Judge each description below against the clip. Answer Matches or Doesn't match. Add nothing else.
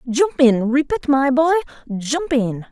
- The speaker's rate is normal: Matches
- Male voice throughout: Doesn't match